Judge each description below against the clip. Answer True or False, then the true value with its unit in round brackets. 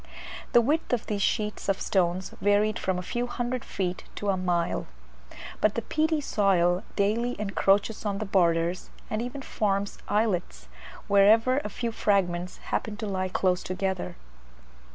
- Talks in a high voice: True (200 Hz)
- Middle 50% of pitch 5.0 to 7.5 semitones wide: False (3.3 semitones)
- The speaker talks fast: False (155 wpm)